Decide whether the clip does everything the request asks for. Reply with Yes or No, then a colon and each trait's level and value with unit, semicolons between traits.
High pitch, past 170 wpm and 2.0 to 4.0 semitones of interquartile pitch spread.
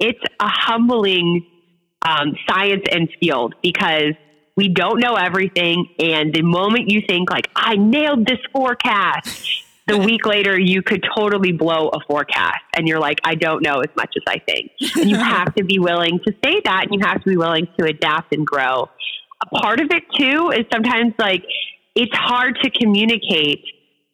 No: high, 195 Hz; average, 180 wpm; average, 5.1 semitones